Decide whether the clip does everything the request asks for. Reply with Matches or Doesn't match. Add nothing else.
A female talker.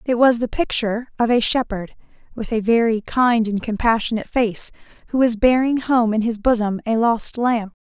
Matches